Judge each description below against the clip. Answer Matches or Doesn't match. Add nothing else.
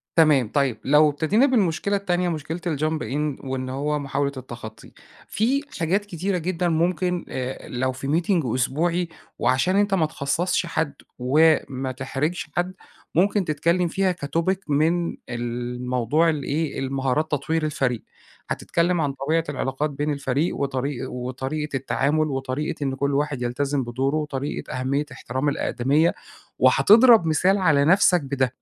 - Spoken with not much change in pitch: Doesn't match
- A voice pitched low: Doesn't match